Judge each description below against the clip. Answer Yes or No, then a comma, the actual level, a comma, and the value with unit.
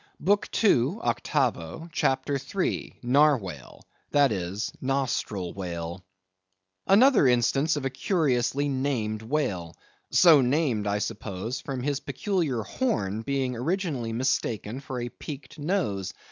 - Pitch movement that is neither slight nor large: No, wide, 6.1 semitones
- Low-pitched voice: Yes, low, 130 Hz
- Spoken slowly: Yes, slow, 115 wpm